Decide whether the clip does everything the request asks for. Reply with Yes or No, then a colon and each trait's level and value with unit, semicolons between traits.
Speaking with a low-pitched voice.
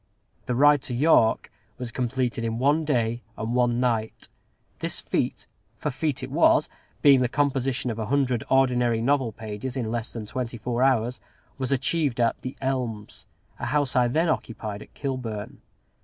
Yes: low, 125 Hz